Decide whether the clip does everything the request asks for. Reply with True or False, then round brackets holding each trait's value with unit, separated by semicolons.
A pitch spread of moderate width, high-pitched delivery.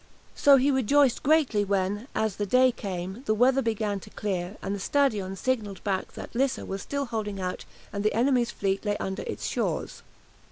True (4.7 semitones; 215 Hz)